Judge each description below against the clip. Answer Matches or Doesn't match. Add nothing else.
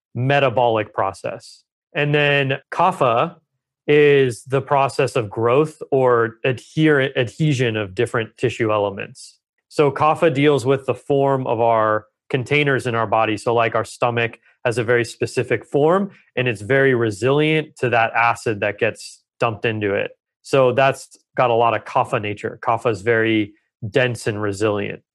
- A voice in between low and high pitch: Doesn't match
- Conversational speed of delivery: Matches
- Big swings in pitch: Doesn't match